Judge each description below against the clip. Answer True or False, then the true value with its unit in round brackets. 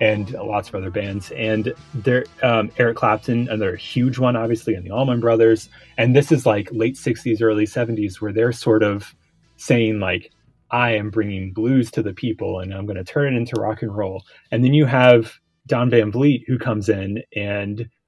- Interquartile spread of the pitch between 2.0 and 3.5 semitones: True (2.5 semitones)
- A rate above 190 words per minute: True (200 wpm)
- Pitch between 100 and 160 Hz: True (115 Hz)